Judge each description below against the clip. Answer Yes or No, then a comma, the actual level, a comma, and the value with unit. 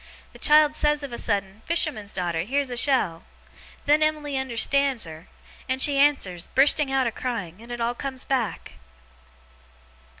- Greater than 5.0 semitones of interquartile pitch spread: Yes, wide, 5.4 semitones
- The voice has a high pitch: Yes, very high, 260 Hz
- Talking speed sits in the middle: Yes, average, 160 wpm